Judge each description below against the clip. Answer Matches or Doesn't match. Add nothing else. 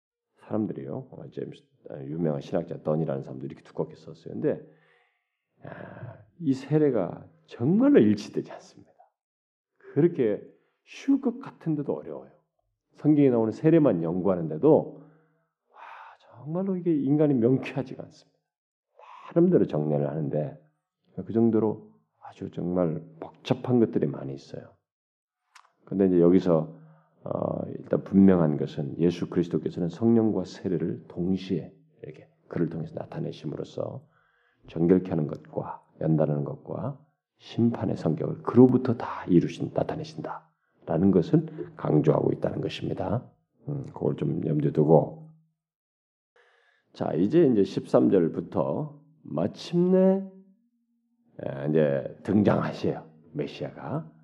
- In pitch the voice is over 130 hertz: Doesn't match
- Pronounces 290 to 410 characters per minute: Doesn't match